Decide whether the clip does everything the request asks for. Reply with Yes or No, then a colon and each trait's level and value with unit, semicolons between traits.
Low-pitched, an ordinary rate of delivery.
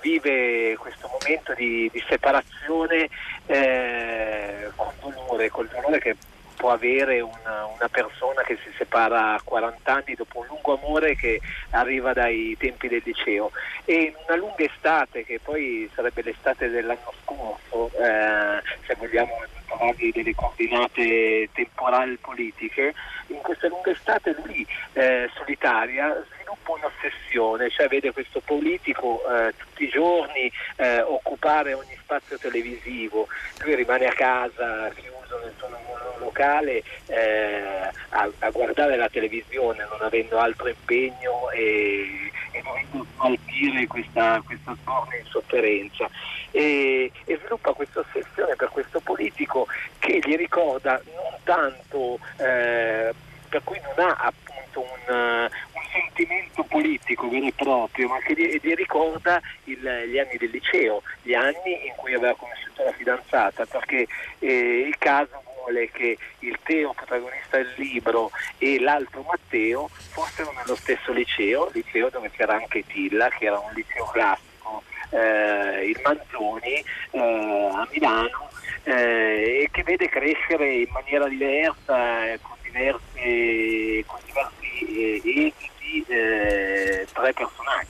Yes: low, 130 Hz; average, 130 wpm